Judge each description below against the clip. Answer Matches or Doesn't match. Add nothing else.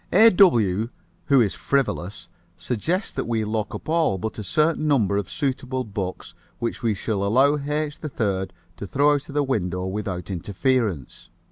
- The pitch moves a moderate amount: Doesn't match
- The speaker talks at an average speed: Matches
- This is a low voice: Matches